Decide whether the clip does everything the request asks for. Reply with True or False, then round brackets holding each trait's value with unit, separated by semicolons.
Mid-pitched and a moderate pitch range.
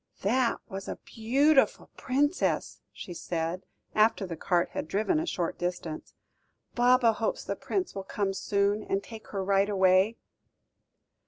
False (200 Hz; 4.1 semitones)